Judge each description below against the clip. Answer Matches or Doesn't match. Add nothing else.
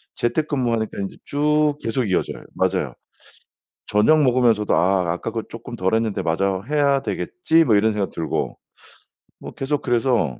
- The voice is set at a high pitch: Doesn't match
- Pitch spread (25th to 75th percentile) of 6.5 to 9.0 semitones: Doesn't match